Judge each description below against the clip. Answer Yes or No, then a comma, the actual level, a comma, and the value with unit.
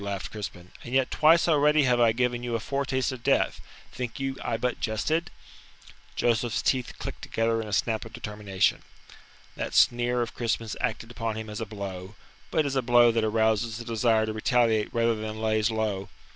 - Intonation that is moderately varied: No, narrow, 2.2 semitones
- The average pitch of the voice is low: Yes, low, 115 Hz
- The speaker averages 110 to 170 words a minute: No, average, 190 wpm